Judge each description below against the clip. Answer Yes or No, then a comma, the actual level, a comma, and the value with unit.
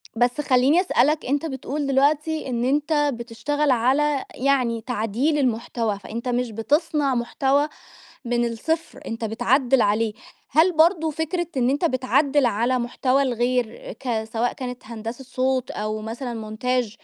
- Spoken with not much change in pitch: No, average, 3.7 semitones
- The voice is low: No, very high, 255 Hz